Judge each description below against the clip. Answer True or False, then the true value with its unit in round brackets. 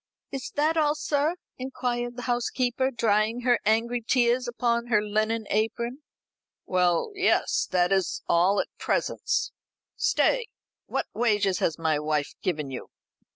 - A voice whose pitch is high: True (235 Hz)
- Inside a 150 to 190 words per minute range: False (135 wpm)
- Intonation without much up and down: False (4.3 semitones)